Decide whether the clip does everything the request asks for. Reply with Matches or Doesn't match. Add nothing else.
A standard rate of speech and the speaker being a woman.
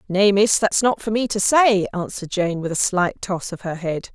Doesn't match